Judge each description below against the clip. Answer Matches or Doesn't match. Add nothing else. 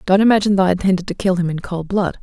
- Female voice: Matches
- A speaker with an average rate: Doesn't match